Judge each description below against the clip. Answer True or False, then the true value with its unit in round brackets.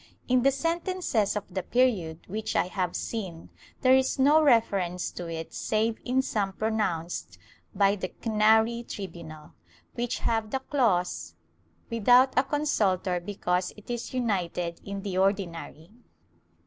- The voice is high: True (210 Hz)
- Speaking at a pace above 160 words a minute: False (135 wpm)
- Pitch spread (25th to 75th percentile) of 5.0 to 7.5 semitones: True (5.3 semitones)